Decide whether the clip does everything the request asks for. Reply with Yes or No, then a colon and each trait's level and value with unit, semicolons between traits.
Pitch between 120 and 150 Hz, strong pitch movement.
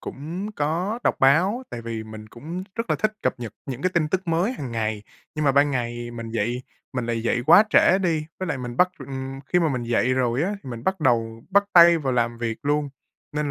Yes: low, 135 Hz; wide, 6.3 semitones